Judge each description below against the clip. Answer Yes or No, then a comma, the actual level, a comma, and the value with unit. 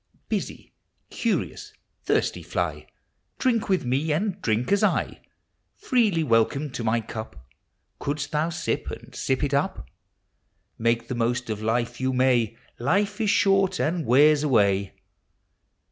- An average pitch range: No, wide, 7.1 semitones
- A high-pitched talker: No, low, 135 Hz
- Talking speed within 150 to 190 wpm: No, slow, 135 wpm